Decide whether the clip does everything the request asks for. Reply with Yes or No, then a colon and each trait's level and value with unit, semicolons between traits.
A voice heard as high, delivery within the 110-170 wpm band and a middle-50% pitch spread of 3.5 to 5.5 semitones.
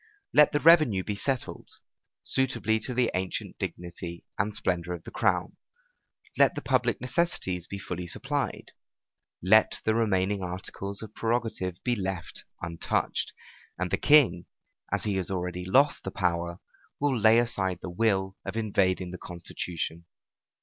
No: very low, 95 Hz; average, 145 wpm; average, 4.1 semitones